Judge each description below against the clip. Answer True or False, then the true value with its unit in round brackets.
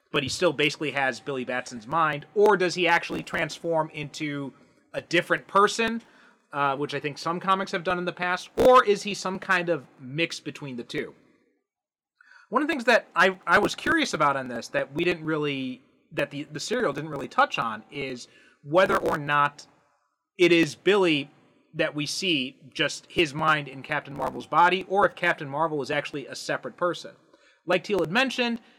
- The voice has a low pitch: False (155 Hz)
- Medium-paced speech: True (190 wpm)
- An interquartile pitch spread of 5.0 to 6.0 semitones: False (4.1 semitones)